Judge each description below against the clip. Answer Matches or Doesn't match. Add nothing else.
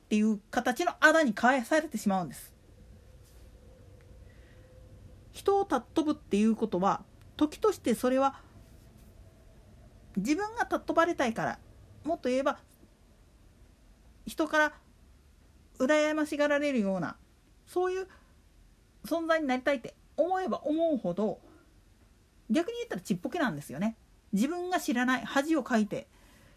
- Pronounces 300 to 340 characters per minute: Doesn't match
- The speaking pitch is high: Matches